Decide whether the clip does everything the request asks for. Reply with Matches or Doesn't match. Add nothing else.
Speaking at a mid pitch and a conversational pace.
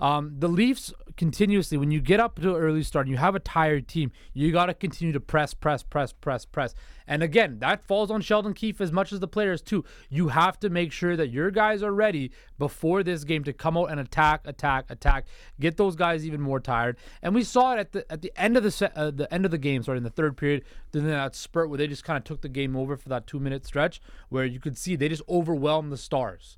Doesn't match